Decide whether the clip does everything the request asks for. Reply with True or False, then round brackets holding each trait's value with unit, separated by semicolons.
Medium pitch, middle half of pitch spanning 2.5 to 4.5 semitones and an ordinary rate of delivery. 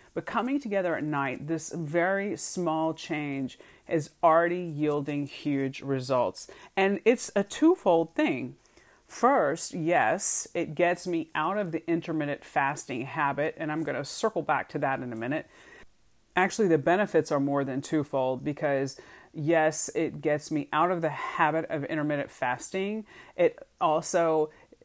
True (160 Hz; 3.3 semitones; 150 wpm)